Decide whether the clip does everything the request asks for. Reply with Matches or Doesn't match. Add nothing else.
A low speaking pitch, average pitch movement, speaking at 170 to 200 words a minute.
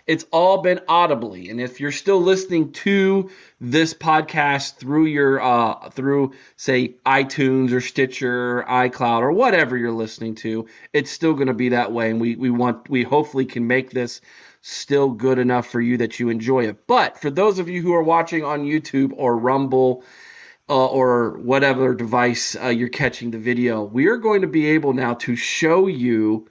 Matches